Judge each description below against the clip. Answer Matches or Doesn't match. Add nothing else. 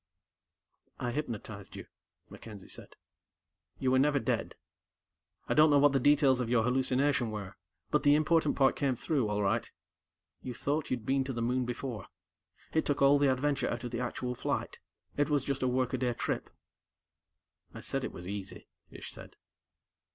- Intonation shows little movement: Doesn't match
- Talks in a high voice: Doesn't match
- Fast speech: Doesn't match